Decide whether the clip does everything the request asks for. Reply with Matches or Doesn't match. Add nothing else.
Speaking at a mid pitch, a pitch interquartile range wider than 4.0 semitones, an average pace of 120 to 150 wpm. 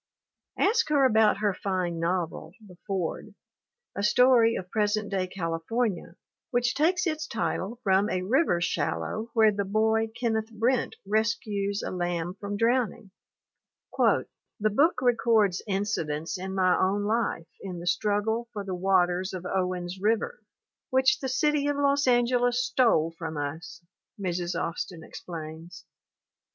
Doesn't match